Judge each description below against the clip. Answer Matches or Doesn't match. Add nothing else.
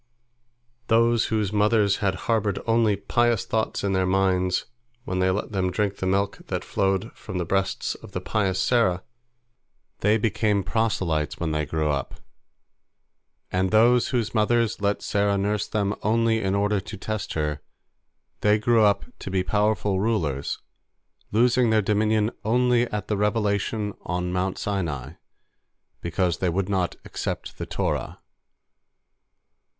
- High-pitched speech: Doesn't match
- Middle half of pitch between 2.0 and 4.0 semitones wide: Matches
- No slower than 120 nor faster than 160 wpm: Matches